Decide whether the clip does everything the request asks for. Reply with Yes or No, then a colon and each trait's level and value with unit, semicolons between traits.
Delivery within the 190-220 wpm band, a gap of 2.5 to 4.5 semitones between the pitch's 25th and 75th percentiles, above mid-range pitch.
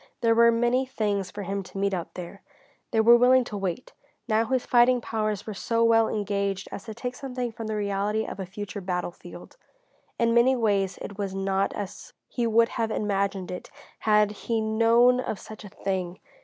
Yes: average, 195 wpm; average, 2.9 semitones; high, 215 Hz